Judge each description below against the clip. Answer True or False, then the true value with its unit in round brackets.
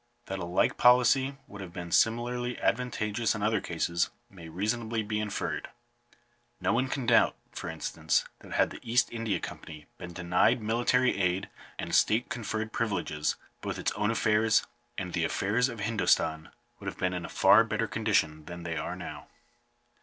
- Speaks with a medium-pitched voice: False (105 Hz)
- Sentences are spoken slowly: False (170 wpm)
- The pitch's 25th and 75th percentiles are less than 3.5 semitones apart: False (4.5 semitones)